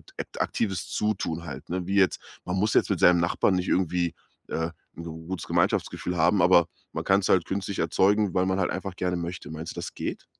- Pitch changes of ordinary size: No, narrow, 2.0 semitones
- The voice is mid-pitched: No, very low, 90 Hz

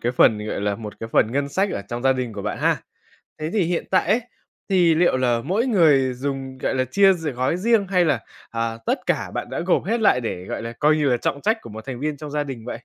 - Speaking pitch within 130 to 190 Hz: Yes, low, 135 Hz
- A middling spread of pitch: No, wide, 6.8 semitones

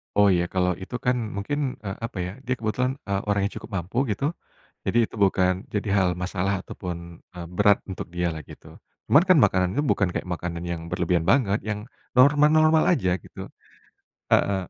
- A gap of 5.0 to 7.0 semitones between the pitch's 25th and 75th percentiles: Yes, average, 5.3 semitones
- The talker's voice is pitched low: Yes, low, 100 Hz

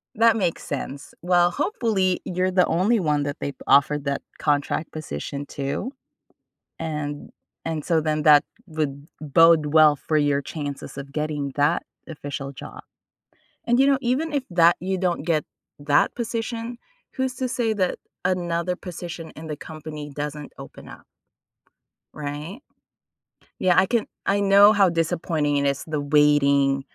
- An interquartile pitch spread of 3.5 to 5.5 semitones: Yes, average, 4.3 semitones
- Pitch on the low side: No, medium, 160 Hz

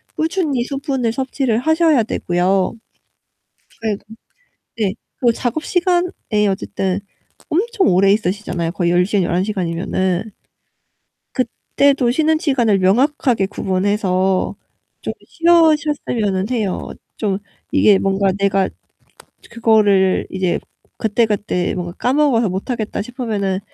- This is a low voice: No, high, 215 Hz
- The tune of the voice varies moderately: No, wide, 5.9 semitones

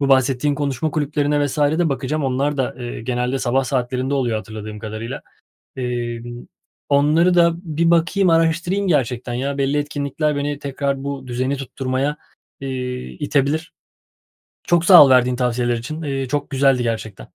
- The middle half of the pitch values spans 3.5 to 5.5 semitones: No, average, 2.9 semitones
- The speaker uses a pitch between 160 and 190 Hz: No, low, 135 Hz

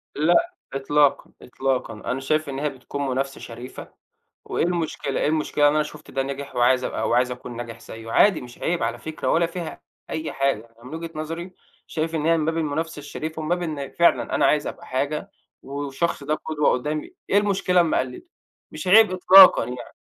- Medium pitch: Yes, medium, 150 Hz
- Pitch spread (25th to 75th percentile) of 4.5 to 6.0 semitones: No, average, 3.6 semitones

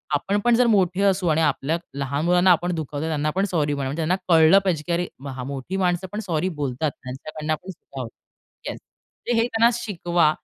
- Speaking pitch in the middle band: Yes, medium, 165 Hz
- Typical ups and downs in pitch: Yes, average, 4.2 semitones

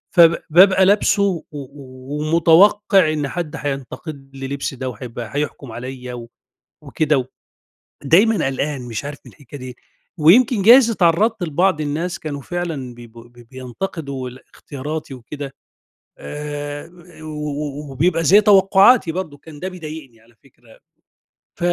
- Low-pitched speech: No, medium, 150 Hz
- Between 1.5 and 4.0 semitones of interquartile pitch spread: No, average, 4.7 semitones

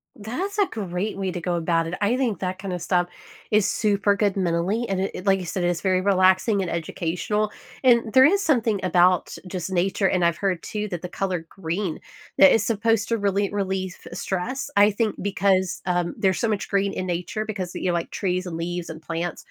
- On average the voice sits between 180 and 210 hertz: Yes, high, 190 Hz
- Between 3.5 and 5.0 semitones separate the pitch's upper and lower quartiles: No, average, 2.8 semitones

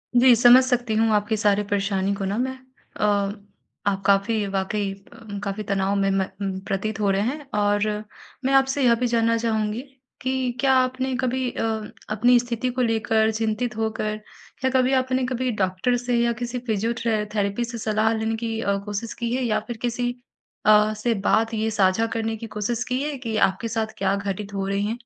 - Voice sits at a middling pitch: No, high, 225 Hz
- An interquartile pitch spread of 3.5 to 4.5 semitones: No, average, 3.0 semitones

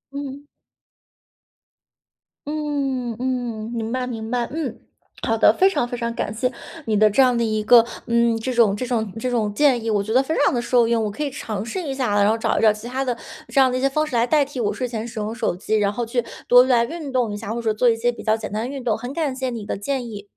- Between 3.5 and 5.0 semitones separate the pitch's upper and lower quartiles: No, average, 2.9 semitones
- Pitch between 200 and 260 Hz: Yes, high, 240 Hz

